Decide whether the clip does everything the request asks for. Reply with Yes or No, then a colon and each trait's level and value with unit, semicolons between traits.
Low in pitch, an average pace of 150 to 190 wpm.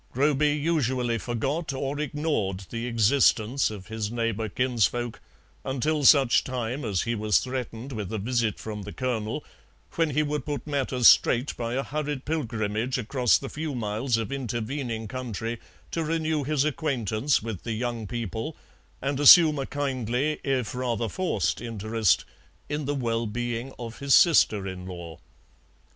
Yes: low, 125 Hz; average, 155 wpm